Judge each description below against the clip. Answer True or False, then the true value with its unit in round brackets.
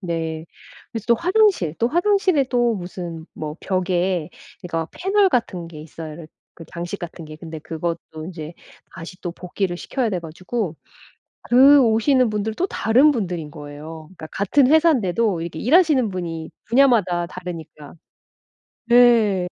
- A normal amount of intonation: False (6.7 semitones)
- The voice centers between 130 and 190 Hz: True (185 Hz)